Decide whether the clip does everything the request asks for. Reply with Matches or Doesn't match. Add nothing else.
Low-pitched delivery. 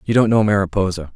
Matches